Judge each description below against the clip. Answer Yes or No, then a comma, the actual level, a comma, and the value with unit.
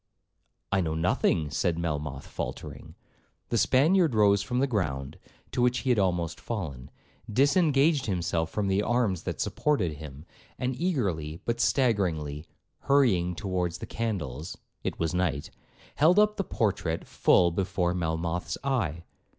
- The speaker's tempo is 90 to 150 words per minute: Yes, average, 140 wpm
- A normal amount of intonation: No, wide, 7.2 semitones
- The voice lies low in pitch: Yes, very low, 95 Hz